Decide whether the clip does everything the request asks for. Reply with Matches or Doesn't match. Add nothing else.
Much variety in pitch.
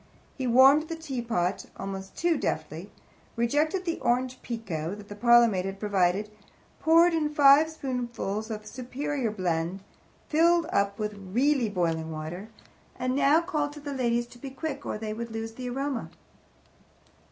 Matches